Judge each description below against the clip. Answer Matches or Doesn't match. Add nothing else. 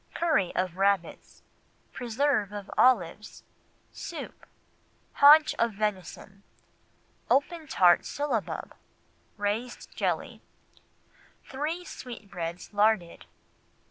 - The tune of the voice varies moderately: Doesn't match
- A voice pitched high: Matches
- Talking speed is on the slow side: Matches